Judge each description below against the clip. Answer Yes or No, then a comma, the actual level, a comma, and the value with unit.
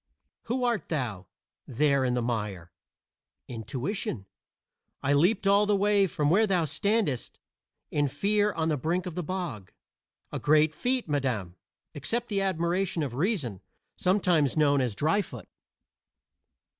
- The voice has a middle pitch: Yes, medium, 160 Hz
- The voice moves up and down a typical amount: No, wide, 7.2 semitones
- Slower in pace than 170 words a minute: Yes, slow, 135 wpm